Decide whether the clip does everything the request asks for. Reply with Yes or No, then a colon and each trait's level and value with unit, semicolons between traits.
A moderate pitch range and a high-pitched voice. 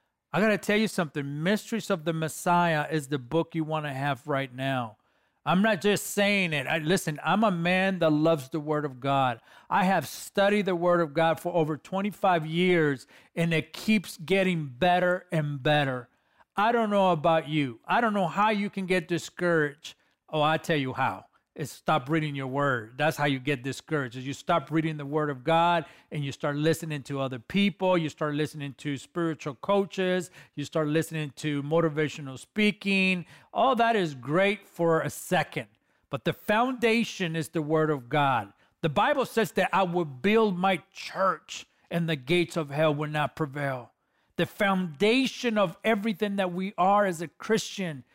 No: average, 4.5 semitones; medium, 165 Hz